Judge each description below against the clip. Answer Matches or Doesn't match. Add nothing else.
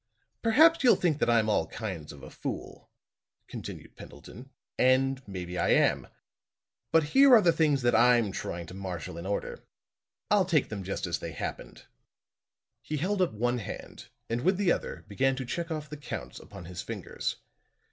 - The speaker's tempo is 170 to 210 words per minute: Matches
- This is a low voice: Matches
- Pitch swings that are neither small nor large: Doesn't match